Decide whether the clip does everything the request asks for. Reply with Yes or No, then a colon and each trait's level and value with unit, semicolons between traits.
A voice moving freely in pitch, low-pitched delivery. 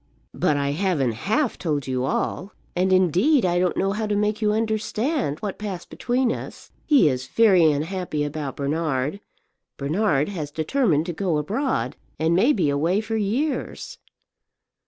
No: wide, 6.3 semitones; medium, 180 Hz